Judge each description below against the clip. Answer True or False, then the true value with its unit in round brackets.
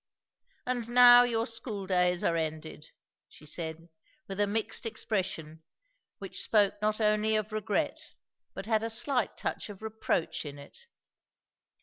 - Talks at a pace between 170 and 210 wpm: False (140 wpm)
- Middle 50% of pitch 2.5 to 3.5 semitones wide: False (4.1 semitones)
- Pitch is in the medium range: False (210 Hz)